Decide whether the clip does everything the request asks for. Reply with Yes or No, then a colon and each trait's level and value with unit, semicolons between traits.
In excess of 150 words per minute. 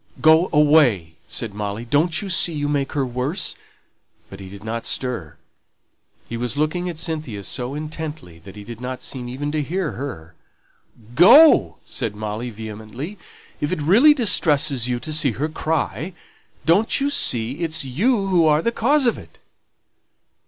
Yes: average, 165 wpm